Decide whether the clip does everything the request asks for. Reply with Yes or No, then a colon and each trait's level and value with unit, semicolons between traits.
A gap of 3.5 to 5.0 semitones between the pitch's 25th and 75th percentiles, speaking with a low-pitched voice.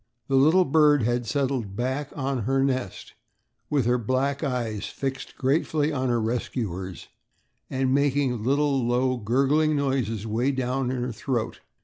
No: narrow, 2.5 semitones; low, 130 Hz